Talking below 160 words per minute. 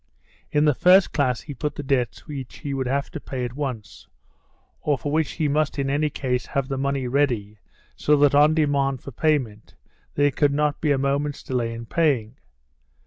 No: average, 195 wpm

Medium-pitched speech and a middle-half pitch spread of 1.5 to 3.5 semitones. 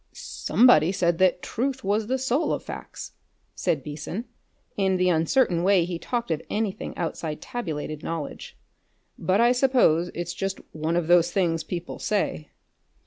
No: medium, 180 Hz; average, 5.1 semitones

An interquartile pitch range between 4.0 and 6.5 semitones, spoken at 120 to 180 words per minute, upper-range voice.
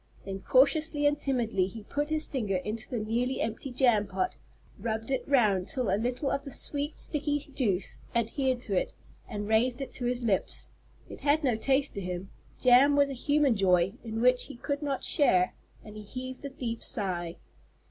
No: average, 4.7 semitones; average, 190 wpm; high, 245 Hz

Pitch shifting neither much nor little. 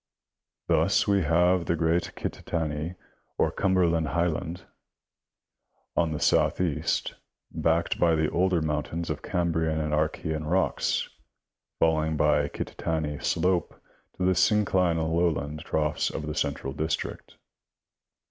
No: narrow, 2.1 semitones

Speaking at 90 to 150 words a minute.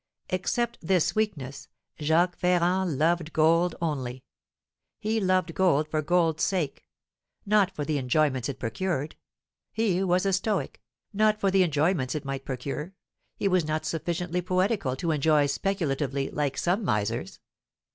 Yes: average, 140 wpm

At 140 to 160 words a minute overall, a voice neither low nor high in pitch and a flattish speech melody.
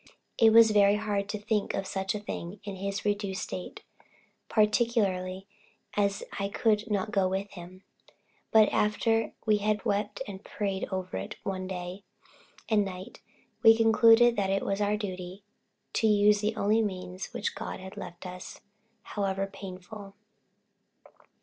No: average, 150 wpm; high, 200 Hz; narrow, 1.9 semitones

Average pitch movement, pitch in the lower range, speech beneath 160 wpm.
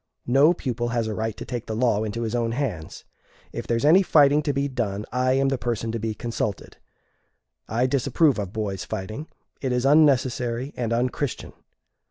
No: average, 3.6 semitones; low, 120 Hz; average, 190 wpm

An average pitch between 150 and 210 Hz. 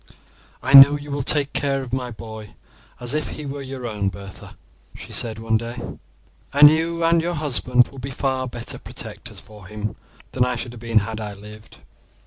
No: low, 125 Hz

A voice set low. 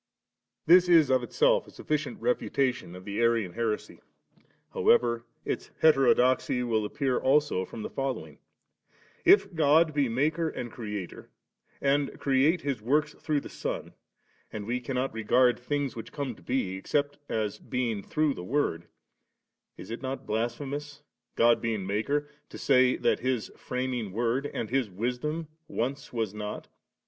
Yes: low, 125 Hz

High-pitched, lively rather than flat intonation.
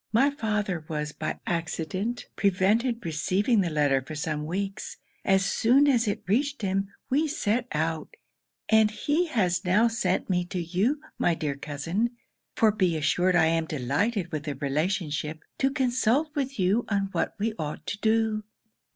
Yes: high, 195 Hz; wide, 5.9 semitones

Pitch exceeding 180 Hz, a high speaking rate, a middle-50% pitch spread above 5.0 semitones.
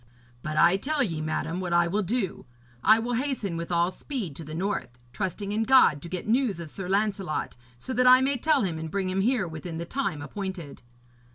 Yes: high, 190 Hz; fast, 215 wpm; wide, 5.4 semitones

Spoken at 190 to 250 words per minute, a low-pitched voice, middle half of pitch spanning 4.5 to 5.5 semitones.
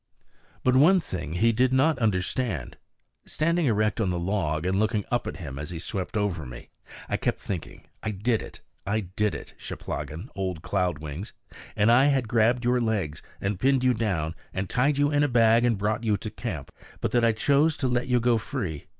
Yes: fast, 205 wpm; low, 110 Hz; average, 5.2 semitones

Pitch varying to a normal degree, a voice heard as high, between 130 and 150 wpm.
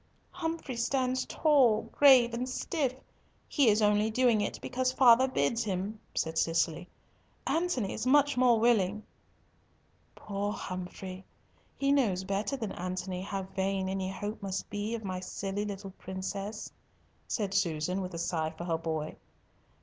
Yes: average, 4.8 semitones; high, 205 Hz; average, 145 wpm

